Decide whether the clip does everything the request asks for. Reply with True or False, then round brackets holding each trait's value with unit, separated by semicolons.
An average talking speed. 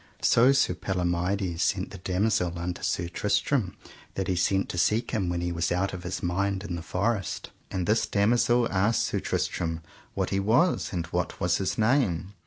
True (190 wpm)